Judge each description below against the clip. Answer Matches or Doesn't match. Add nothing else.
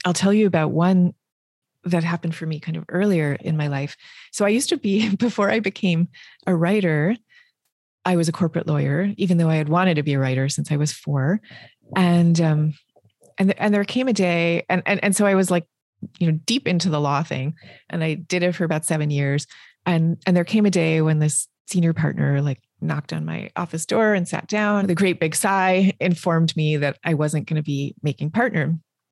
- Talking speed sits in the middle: Doesn't match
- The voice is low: Doesn't match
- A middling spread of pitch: Matches